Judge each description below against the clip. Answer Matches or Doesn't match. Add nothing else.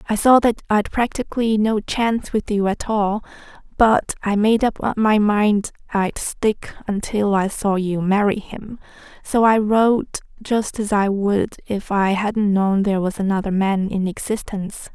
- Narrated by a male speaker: Doesn't match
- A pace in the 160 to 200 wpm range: Matches